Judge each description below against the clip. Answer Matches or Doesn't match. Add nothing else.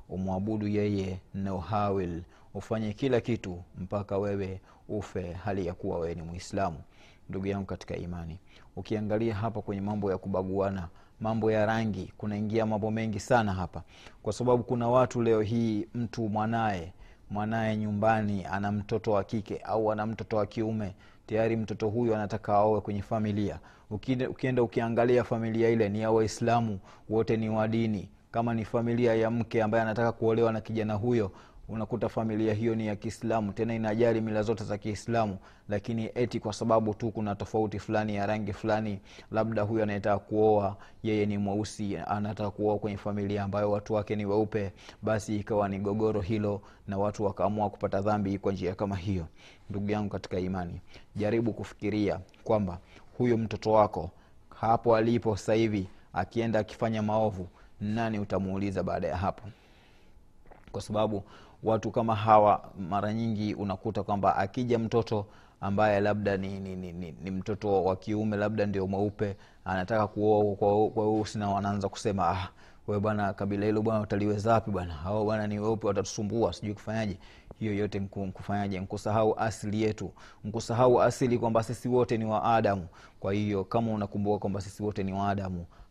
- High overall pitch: Doesn't match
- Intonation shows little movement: Matches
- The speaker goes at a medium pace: Matches